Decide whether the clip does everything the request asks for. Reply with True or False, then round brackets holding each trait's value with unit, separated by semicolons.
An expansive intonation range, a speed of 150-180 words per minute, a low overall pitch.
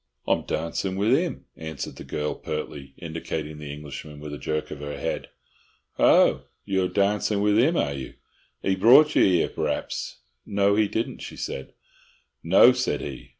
True (5.9 semitones; 165 wpm; 90 Hz)